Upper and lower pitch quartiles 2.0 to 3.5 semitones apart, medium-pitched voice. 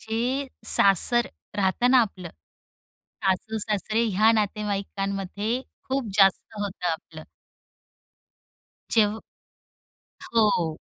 No: average, 2.7 semitones; high, 210 Hz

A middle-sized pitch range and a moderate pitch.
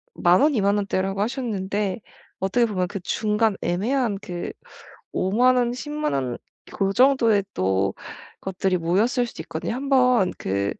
No: average, 4.9 semitones; high, 205 Hz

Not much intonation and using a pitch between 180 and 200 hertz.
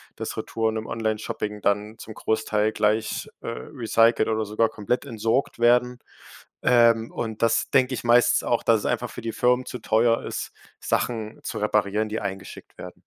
No: narrow, 1.7 semitones; low, 110 Hz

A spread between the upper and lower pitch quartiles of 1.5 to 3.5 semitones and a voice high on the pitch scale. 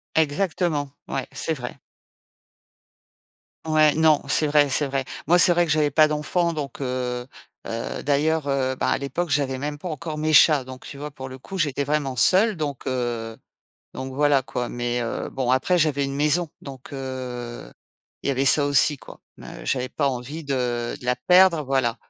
No: average, 3.0 semitones; medium, 140 Hz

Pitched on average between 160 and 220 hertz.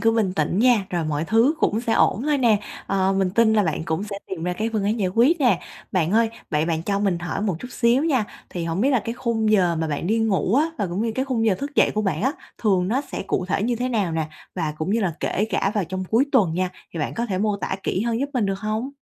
Yes: high, 205 Hz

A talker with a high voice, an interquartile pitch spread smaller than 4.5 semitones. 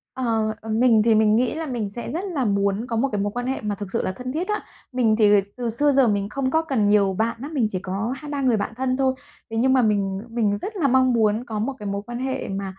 Yes: high, 230 Hz; average, 3.9 semitones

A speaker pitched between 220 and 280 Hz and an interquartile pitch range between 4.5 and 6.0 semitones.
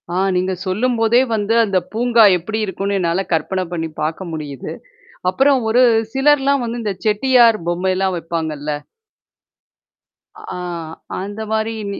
No: high, 200 Hz; average, 4.8 semitones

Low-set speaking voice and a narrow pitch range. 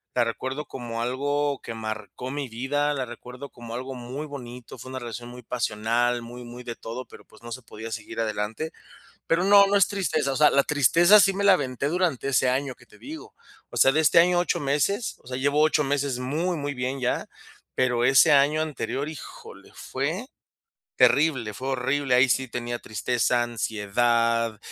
No: low, 130 Hz; average, 3.4 semitones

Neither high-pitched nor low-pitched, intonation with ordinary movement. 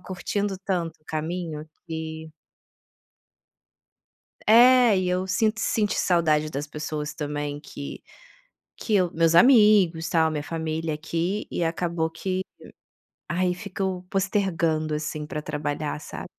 Yes: medium, 165 Hz; average, 3.5 semitones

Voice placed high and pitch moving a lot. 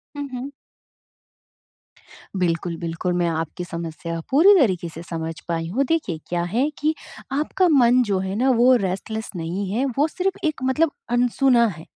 Yes: high, 200 Hz; wide, 8.0 semitones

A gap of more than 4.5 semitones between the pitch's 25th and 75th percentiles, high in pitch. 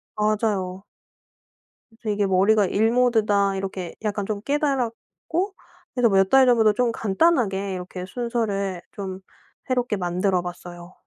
No: average, 3.6 semitones; high, 205 Hz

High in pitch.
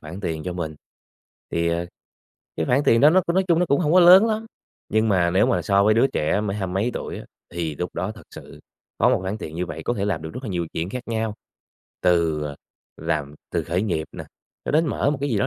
No: low, 100 Hz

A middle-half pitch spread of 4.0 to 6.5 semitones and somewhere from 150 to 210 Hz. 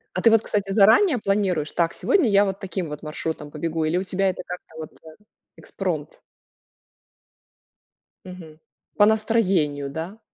Yes: average, 4.5 semitones; medium, 185 Hz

